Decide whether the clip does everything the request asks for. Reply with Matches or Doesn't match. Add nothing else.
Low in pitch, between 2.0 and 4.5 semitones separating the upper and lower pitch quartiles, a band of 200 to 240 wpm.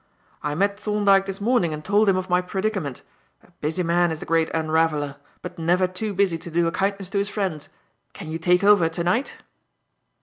Doesn't match